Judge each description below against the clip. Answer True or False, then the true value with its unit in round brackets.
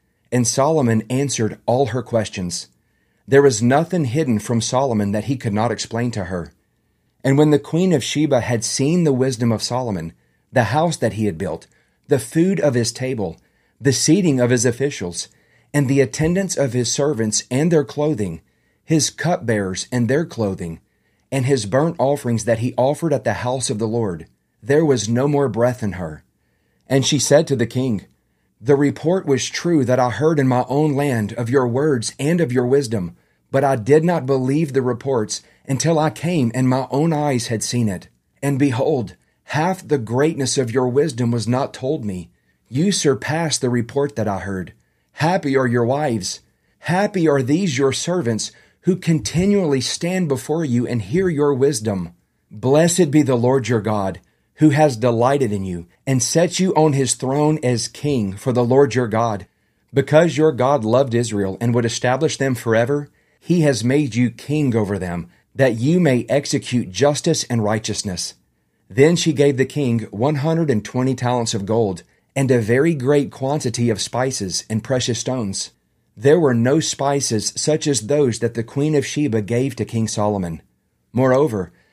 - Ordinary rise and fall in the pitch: True (4.6 semitones)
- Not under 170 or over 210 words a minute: True (180 wpm)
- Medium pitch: False (130 Hz)